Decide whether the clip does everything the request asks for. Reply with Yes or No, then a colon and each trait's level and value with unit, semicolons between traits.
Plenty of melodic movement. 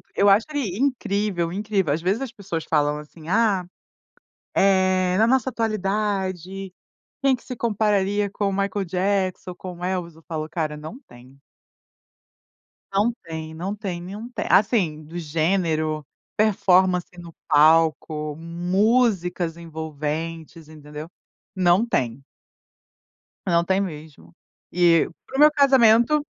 No: average, 4.3 semitones